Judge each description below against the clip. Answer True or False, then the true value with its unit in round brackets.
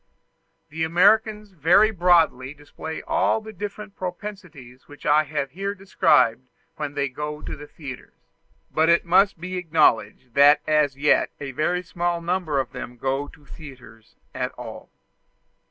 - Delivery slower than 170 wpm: True (150 wpm)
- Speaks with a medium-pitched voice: True (155 Hz)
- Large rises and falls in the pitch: False (4.4 semitones)